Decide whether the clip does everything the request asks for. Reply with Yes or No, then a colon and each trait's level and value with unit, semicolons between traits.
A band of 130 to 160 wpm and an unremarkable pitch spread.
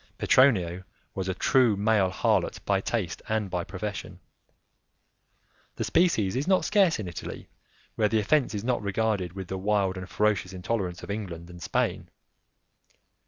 Yes: average, 155 wpm; average, 3.3 semitones